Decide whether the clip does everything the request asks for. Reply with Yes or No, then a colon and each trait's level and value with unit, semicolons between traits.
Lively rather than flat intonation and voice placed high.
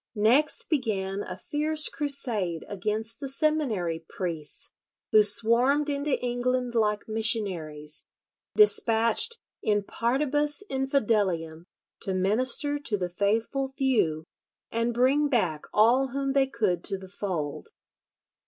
Yes: wide, 5.9 semitones; high, 230 Hz